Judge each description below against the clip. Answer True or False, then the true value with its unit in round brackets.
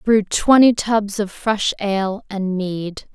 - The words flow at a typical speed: True (155 wpm)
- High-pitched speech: True (205 Hz)